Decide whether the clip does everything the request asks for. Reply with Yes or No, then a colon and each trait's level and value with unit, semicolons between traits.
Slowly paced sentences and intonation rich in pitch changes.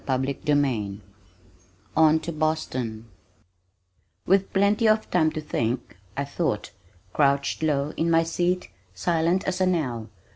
No: slow, 125 wpm; average, 4.7 semitones